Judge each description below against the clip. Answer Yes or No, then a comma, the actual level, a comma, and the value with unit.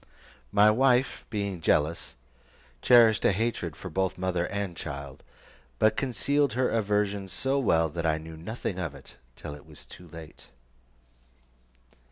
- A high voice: No, very low, 95 Hz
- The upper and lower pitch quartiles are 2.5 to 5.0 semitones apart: No, wide, 5.4 semitones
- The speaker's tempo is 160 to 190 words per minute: No, average, 145 wpm